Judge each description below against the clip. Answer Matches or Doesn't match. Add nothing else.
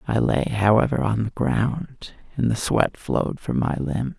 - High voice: Doesn't match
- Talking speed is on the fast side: Doesn't match